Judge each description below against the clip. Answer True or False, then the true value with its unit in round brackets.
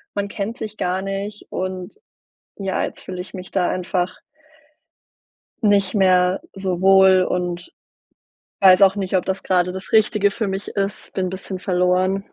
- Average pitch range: False (1.4 semitones)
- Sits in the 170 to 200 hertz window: True (190 Hz)